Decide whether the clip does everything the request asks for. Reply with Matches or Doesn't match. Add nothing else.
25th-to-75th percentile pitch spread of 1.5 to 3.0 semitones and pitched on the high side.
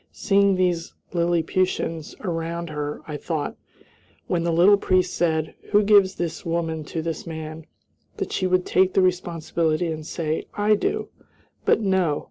Doesn't match